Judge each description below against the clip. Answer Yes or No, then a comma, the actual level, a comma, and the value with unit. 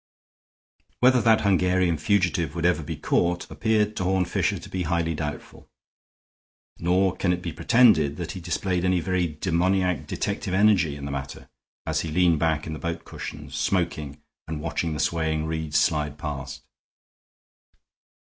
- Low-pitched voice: Yes, very low, 85 Hz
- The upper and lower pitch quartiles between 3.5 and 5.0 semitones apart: No, average, 3.1 semitones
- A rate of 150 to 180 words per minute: Yes, average, 160 wpm